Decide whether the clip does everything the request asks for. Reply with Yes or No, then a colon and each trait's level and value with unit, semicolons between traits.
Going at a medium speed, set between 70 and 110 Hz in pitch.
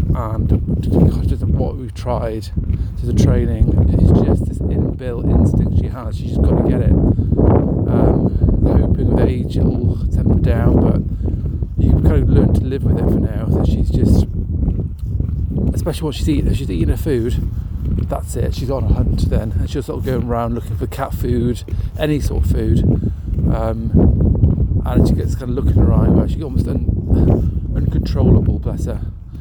Yes: average, 180 wpm; very low, 95 Hz